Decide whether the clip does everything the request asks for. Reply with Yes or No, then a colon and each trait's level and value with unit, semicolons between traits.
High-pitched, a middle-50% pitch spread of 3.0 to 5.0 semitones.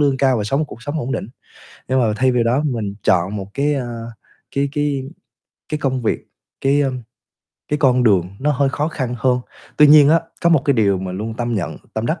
No: low, 130 Hz; average, 4.2 semitones